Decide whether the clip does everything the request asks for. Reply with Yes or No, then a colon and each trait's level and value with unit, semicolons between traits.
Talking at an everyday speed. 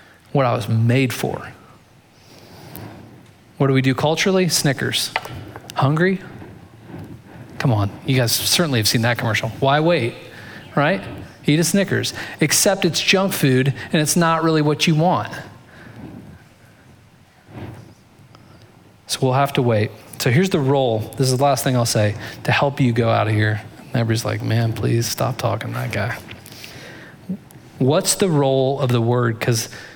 Yes: average, 155 wpm